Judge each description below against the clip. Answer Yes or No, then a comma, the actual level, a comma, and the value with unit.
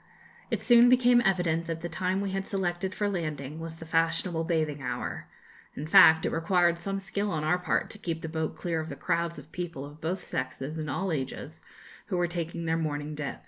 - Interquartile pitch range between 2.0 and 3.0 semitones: Yes, average, 2.7 semitones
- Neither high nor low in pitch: Yes, medium, 165 Hz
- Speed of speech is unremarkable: No, fast, 215 wpm